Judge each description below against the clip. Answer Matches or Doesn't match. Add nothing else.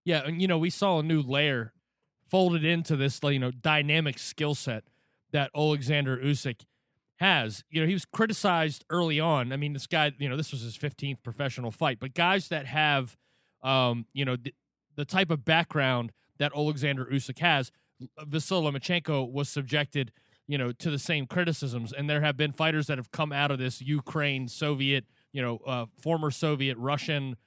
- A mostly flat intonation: Doesn't match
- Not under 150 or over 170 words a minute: Doesn't match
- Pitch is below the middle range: Doesn't match